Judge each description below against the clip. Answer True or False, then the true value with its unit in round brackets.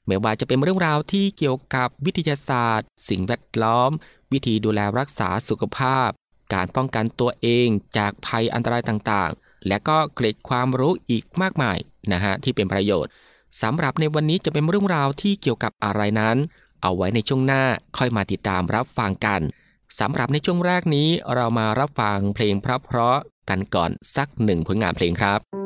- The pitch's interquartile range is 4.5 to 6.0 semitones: True (5.1 semitones)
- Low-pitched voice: True (120 Hz)